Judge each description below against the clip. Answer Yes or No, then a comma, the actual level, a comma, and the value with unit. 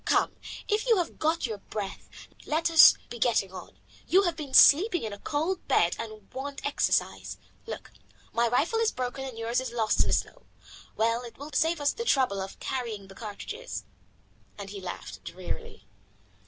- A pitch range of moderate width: No, wide, 7.1 semitones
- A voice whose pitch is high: Yes, very high, 255 Hz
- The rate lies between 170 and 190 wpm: Yes, average, 180 wpm